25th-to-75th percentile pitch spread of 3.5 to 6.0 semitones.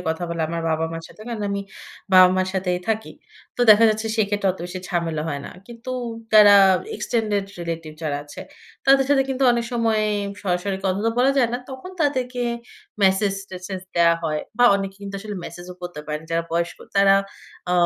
Yes: average, 4.5 semitones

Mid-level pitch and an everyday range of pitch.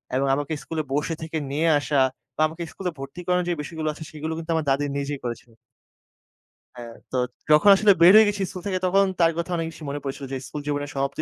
Yes: medium, 155 Hz; average, 3.4 semitones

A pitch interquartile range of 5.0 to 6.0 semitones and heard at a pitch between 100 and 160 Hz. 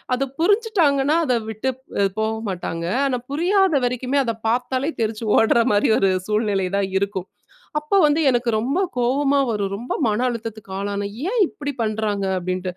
No: wide, 5.4 semitones; high, 235 Hz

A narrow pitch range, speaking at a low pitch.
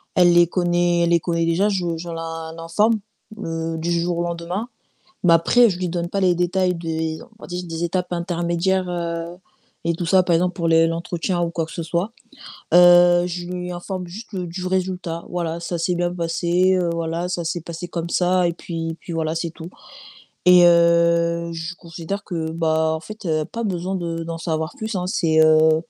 No: narrow, 1.4 semitones; medium, 170 Hz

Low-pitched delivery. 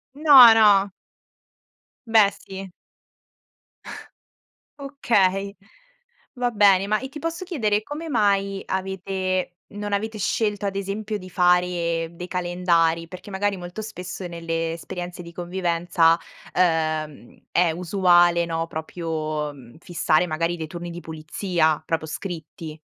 No: medium, 180 Hz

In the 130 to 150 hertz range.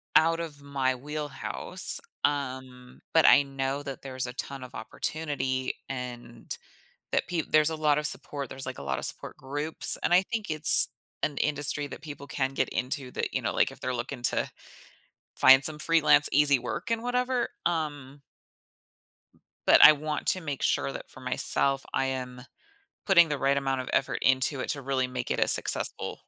Yes: medium, 140 Hz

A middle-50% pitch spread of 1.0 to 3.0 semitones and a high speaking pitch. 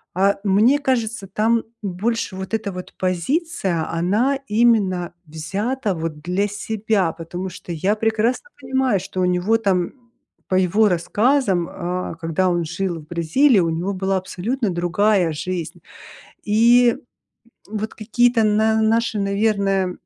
No: average, 3.8 semitones; high, 200 Hz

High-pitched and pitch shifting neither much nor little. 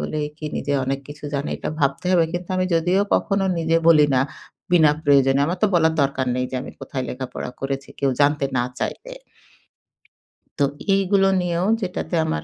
No: medium, 155 Hz; average, 4.4 semitones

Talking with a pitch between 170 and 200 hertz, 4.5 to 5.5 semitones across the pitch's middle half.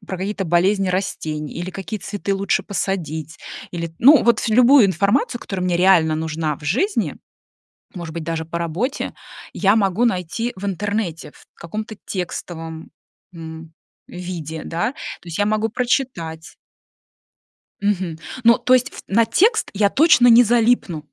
Yes: high, 190 Hz; average, 5.1 semitones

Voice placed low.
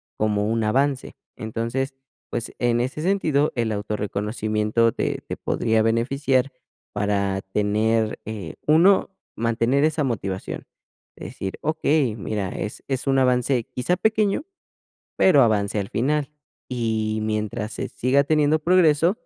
Yes: low, 120 Hz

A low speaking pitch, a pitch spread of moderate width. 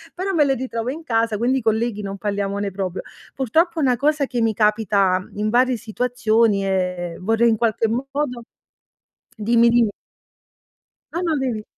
No: high, 230 Hz; average, 3.6 semitones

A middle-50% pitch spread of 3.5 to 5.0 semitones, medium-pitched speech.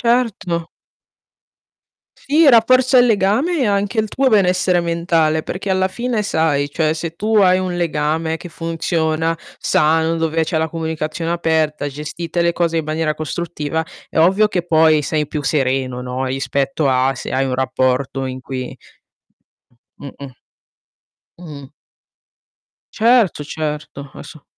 Yes: average, 3.8 semitones; medium, 160 Hz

